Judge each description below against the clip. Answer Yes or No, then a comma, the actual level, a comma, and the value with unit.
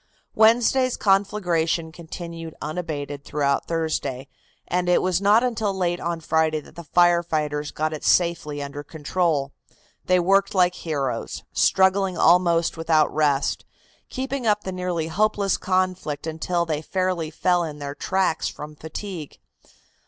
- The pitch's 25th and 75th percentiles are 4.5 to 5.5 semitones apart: No, average, 3.2 semitones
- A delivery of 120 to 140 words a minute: Yes, slow, 135 wpm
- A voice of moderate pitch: Yes, medium, 170 Hz